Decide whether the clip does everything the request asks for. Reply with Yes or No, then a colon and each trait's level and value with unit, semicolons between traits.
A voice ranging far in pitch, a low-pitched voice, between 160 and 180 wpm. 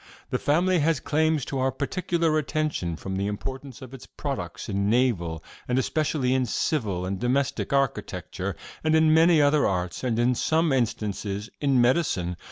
Yes: wide, 7.1 semitones; low, 130 Hz; average, 165 wpm